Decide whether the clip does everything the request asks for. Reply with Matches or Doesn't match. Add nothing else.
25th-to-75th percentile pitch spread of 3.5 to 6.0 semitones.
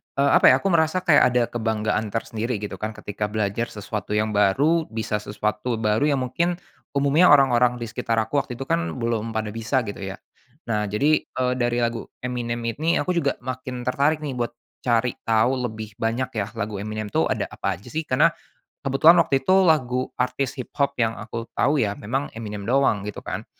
Matches